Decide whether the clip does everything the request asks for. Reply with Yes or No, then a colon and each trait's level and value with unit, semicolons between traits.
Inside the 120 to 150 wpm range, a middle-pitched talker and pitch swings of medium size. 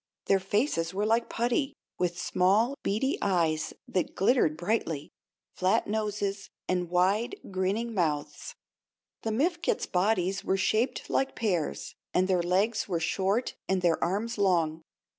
No: slow, 135 wpm; high, 195 Hz; average, 3.7 semitones